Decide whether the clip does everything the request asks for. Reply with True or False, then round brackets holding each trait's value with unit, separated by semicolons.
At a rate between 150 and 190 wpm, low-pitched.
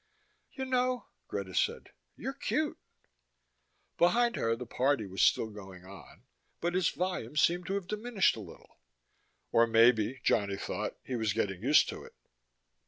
True (155 wpm; 125 Hz)